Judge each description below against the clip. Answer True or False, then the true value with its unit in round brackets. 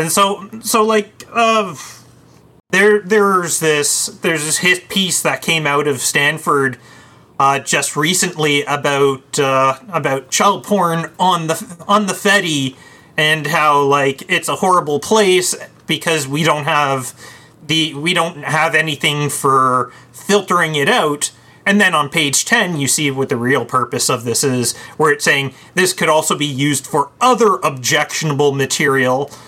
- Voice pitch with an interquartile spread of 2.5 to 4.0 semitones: False (4.4 semitones)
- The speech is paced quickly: False (155 wpm)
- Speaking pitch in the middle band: True (155 Hz)